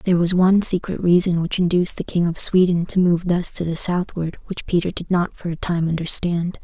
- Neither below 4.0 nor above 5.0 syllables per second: No, 5.5 syllables/s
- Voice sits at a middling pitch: Yes, medium, 175 Hz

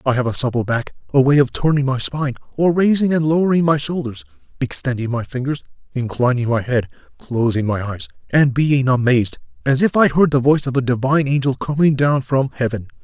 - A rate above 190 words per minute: Yes, average, 200 wpm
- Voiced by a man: Yes, male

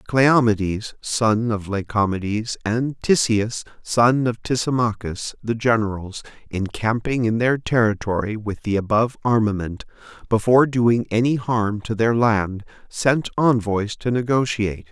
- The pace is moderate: No, slow, 120 wpm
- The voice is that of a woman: No, male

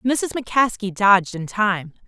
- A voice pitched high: Yes, high, 210 Hz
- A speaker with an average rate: Yes, average, 145 wpm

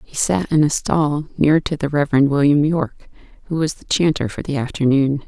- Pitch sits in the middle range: Yes, medium, 145 Hz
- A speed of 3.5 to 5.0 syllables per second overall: No, 5.4 syllables/s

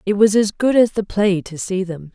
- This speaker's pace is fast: Yes, fast, 280 wpm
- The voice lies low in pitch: No, high, 195 Hz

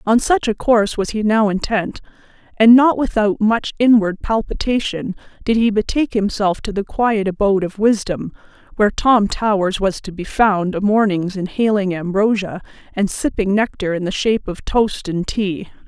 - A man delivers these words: No, female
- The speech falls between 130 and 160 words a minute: No, average, 170 wpm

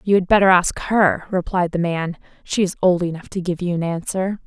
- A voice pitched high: No, medium, 180 Hz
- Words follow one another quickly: Yes, fast, 230 wpm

